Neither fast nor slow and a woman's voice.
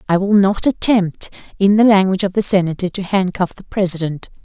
Yes: average, 190 wpm; female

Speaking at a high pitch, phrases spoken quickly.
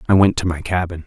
No: very low, 90 Hz; fast, 280 wpm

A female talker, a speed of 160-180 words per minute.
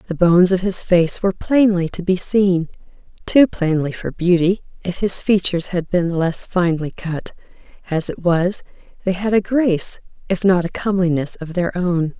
Yes: female; average, 170 wpm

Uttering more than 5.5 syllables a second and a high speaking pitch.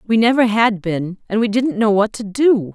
No: 4.7 syllables/s; high, 215 Hz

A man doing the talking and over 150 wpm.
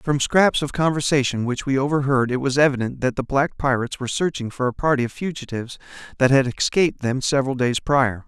Yes: male; fast, 205 wpm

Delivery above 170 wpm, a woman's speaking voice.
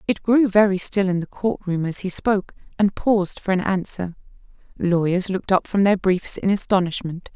Yes: average, 195 wpm; female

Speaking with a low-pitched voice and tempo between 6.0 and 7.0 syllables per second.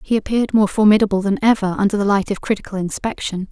No: high, 205 Hz; 6.9 syllables/s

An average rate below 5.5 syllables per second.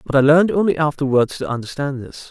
No: 6.4 syllables/s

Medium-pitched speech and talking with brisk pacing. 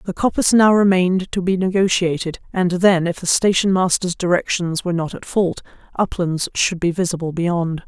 No: medium, 180 Hz; average, 175 wpm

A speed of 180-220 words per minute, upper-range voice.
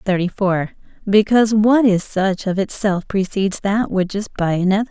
No: average, 170 wpm; high, 200 Hz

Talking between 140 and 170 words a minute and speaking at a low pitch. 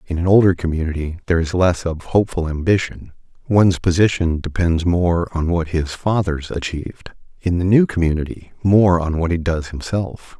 Yes: average, 165 wpm; very low, 85 Hz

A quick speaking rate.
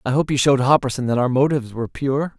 Yes: fast, 250 wpm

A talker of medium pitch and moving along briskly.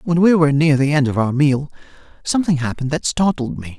Yes: medium, 145 Hz; fast, 220 wpm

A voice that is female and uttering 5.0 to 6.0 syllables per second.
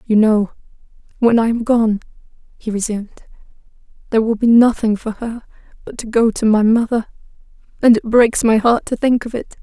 Yes: female; 5.3 syllables/s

